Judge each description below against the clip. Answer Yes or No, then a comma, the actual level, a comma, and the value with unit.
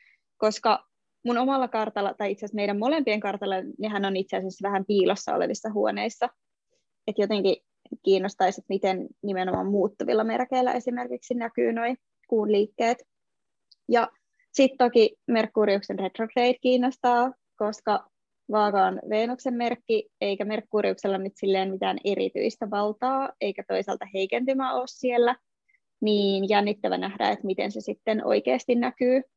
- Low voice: No, high, 220 Hz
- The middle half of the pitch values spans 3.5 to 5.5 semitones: Yes, average, 3.8 semitones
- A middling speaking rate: Yes, average, 130 wpm